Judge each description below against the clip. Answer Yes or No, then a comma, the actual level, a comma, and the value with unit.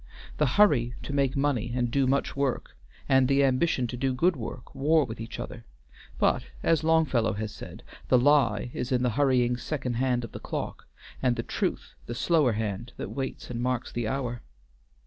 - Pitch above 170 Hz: No, low, 130 Hz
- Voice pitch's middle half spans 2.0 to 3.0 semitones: Yes, narrow, 2.6 semitones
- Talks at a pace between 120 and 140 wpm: No, average, 185 wpm